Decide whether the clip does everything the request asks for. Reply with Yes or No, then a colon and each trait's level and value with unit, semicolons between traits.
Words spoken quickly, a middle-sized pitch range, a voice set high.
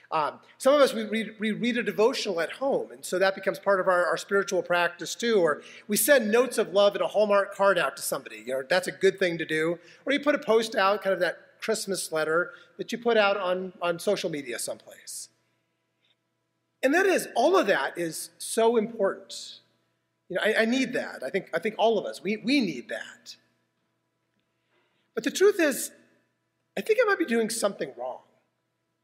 Yes: fast, 210 wpm; average, 4.1 semitones; high, 200 Hz